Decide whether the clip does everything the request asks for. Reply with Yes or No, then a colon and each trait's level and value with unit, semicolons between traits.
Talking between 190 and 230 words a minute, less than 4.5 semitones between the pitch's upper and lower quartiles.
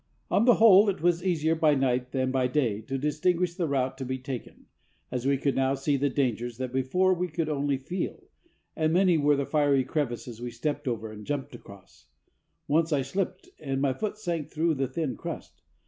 Yes: fast, 205 wpm; average, 4.0 semitones